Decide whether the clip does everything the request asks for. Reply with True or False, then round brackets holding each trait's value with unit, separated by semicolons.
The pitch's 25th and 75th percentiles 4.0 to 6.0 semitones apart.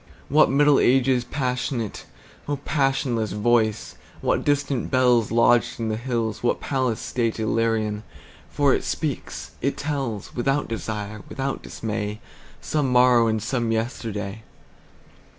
False (3.3 semitones)